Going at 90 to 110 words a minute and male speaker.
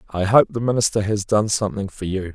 No: fast, 230 wpm; male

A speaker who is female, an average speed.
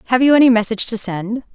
No: female; fast, 235 wpm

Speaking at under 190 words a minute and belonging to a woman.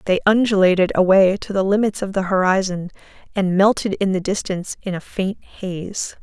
Yes: average, 175 wpm; female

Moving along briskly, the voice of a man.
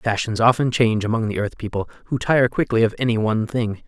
Yes: fast, 215 wpm; male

